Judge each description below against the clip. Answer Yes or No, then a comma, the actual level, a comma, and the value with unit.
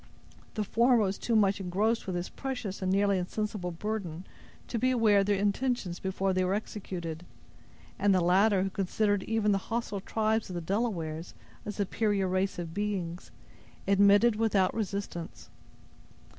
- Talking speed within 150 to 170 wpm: Yes, average, 155 wpm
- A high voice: Yes, high, 200 Hz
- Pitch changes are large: No, narrow, 2.6 semitones